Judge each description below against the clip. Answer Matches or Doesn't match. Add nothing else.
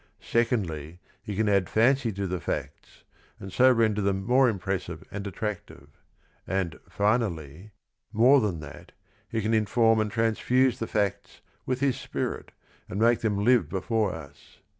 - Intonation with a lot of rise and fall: Doesn't match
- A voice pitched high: Doesn't match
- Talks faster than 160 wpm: Doesn't match